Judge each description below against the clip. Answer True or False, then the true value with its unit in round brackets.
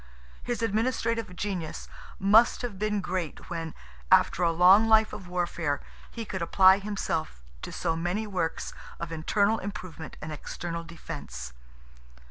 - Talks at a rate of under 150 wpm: True (135 wpm)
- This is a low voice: False (185 Hz)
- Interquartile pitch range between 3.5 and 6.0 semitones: True (4.1 semitones)